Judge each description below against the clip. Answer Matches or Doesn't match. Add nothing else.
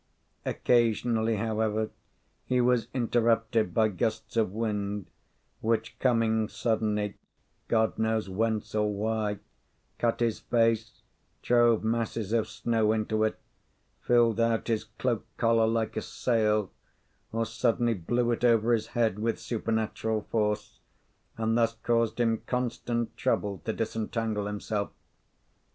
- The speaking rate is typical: Doesn't match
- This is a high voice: Doesn't match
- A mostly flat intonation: Matches